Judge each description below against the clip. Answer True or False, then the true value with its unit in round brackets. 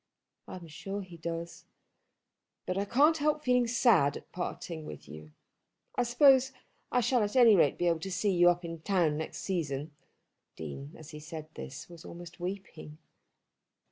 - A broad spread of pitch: True (6.0 semitones)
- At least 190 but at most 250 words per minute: False (175 wpm)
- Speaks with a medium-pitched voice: True (175 Hz)